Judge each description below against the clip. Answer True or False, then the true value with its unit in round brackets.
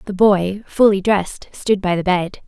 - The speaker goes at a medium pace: True (195 wpm)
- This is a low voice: False (195 Hz)